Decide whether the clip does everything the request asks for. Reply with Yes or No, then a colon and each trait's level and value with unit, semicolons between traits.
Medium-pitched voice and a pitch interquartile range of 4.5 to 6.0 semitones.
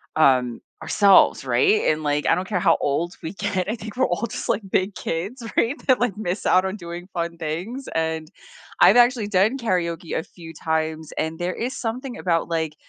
Yes: medium, 180 Hz; wide, 5.4 semitones